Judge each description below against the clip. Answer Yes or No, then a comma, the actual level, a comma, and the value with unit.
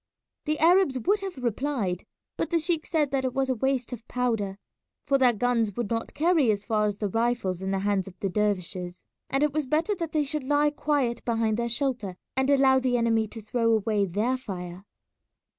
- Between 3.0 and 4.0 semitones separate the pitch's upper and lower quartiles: No, average, 5.2 semitones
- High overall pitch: Yes, high, 240 Hz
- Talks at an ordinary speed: No, fast, 210 wpm